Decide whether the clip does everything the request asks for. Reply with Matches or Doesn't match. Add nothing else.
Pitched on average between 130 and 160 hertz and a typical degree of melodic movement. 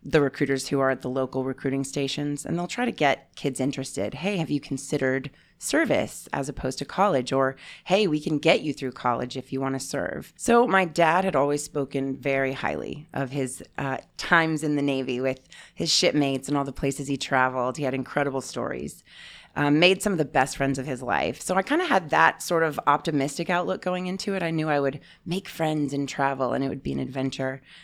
Matches